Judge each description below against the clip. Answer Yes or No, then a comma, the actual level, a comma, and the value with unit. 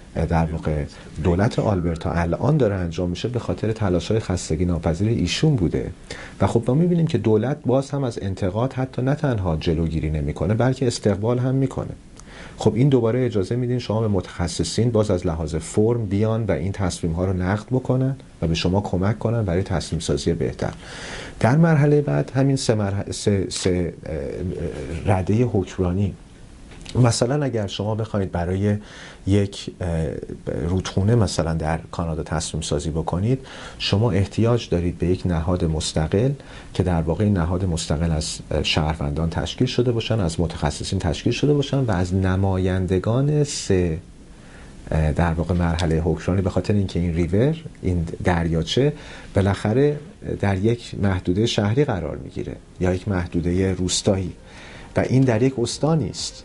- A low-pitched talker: Yes, very low, 95 Hz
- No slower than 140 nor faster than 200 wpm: Yes, average, 150 wpm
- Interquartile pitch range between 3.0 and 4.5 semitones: No, wide, 5.5 semitones